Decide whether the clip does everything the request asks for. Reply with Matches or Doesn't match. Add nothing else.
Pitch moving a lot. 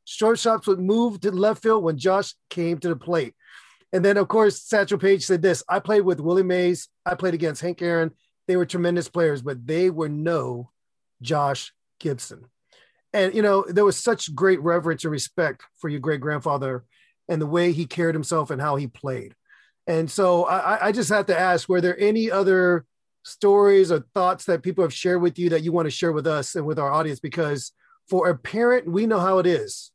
Doesn't match